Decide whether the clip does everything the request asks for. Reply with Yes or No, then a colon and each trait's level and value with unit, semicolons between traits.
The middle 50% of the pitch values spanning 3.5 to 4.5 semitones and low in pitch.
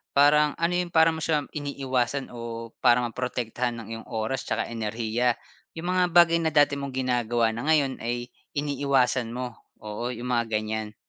Yes: average, 3.8 semitones; low, 125 Hz